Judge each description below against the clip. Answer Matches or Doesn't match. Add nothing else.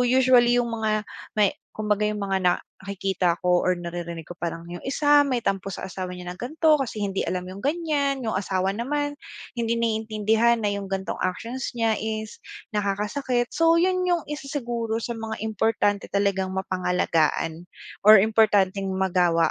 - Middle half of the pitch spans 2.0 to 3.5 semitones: Doesn't match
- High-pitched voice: Matches